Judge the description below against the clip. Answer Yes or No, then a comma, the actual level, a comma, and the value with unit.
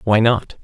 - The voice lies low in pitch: Yes, low, 110 Hz